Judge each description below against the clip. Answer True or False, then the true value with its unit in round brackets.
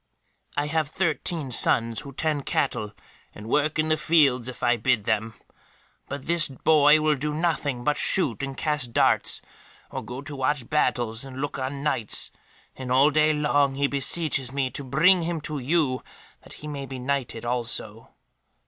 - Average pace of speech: True (175 wpm)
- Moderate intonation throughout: True (3.3 semitones)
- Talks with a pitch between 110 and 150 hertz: True (140 Hz)